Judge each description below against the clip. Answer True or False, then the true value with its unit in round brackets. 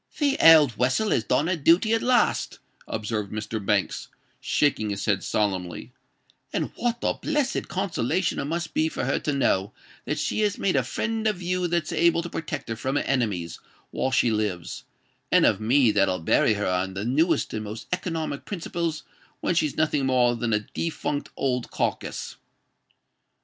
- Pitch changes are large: True (8.0 semitones)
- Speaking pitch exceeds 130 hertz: True (140 Hz)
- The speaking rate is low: False (175 wpm)